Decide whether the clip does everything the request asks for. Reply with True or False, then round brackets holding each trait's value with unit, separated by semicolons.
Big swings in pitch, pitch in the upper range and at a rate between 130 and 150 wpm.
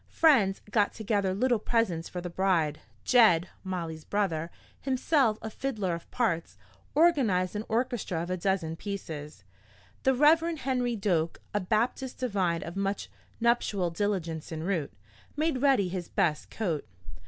True (6.0 semitones; 200 Hz; 140 wpm)